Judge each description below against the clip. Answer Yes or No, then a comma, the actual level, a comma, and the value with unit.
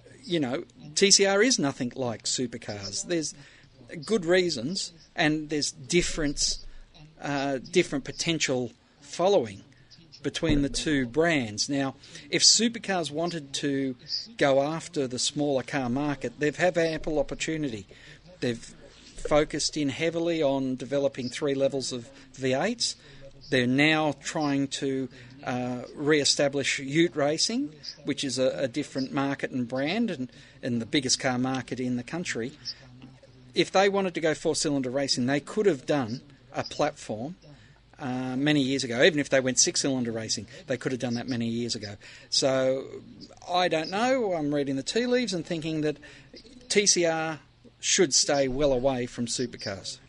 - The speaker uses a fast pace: No, average, 150 wpm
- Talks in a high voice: No, medium, 140 Hz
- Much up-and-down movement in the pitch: No, average, 3.5 semitones